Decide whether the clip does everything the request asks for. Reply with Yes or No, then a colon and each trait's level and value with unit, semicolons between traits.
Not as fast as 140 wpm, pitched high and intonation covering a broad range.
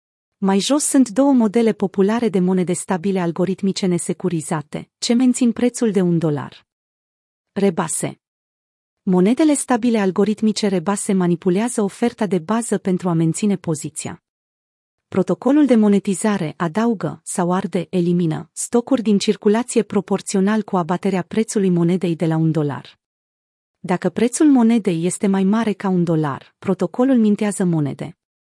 No: average, 130 wpm; high, 195 Hz; average, 4.0 semitones